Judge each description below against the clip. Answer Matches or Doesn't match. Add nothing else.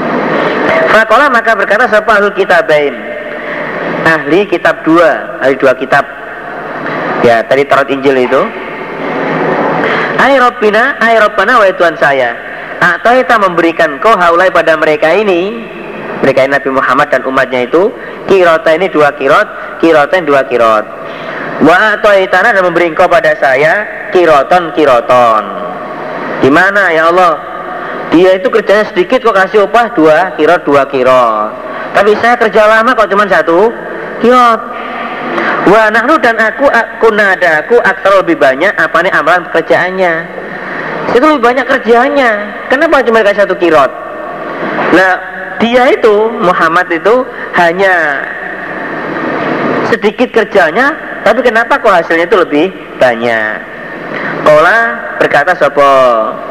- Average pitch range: Doesn't match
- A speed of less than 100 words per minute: Doesn't match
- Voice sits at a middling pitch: Doesn't match